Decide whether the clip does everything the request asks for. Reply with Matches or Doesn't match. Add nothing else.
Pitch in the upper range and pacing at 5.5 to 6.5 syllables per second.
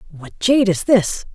Doesn't match